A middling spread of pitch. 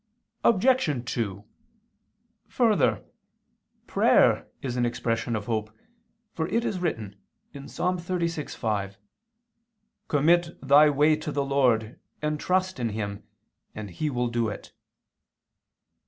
No: wide, 6.4 semitones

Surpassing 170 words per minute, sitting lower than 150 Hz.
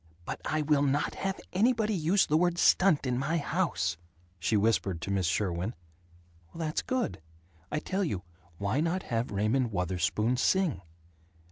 No: average, 150 wpm; medium, 140 Hz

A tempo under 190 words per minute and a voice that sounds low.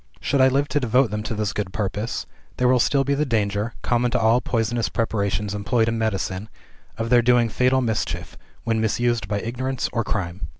No: average, 200 wpm; low, 115 Hz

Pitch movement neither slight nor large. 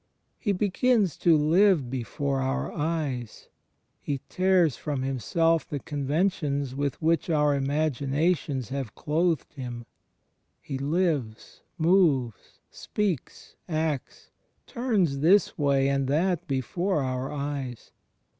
Yes: average, 4.1 semitones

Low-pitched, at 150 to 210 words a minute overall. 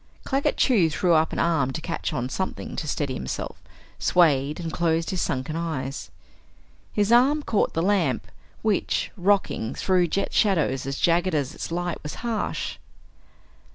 No: medium, 170 Hz; average, 155 wpm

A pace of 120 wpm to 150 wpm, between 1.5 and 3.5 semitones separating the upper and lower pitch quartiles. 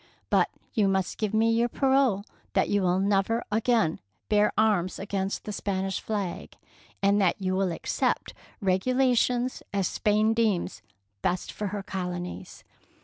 Yes: average, 145 wpm; average, 2.8 semitones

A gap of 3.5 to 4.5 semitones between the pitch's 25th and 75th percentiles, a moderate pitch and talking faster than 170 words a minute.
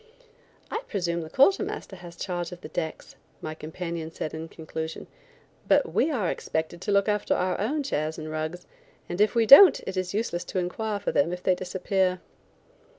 Yes: average, 4.0 semitones; medium, 180 Hz; average, 190 wpm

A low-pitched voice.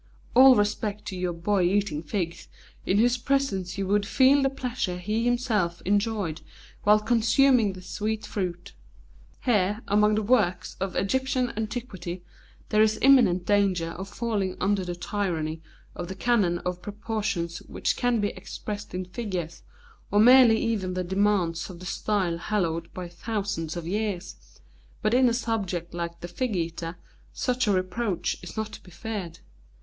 No: high, 205 Hz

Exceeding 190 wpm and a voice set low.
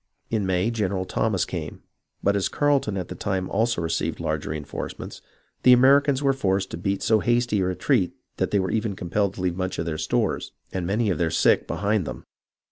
Yes: fast, 205 wpm; low, 100 Hz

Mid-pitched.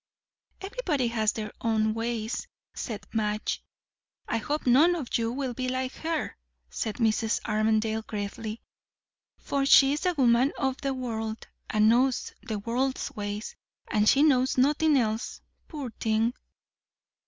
No: high, 235 Hz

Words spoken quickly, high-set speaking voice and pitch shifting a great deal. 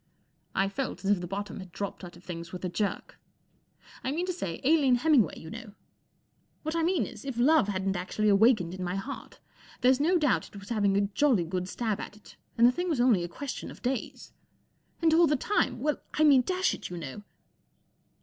Yes: fast, 215 wpm; high, 220 Hz; wide, 7.2 semitones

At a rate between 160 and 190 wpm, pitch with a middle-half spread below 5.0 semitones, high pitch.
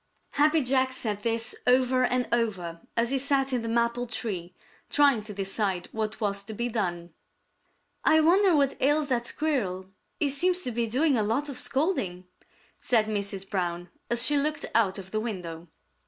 No: average, 175 wpm; wide, 5.4 semitones; high, 235 Hz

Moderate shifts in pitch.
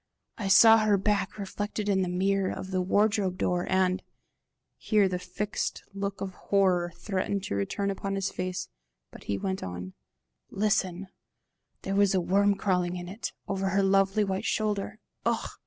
No: narrow, 1.6 semitones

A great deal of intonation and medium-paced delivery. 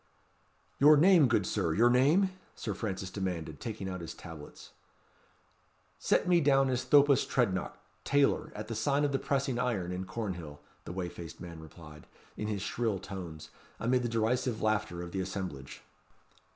Yes: wide, 6.1 semitones; average, 165 wpm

